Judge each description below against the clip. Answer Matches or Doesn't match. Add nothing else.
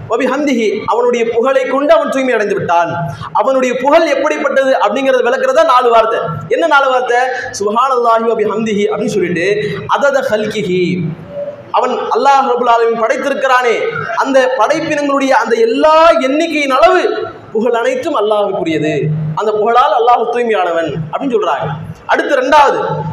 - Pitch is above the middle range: Matches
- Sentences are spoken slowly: Matches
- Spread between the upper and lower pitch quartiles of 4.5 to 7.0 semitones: Matches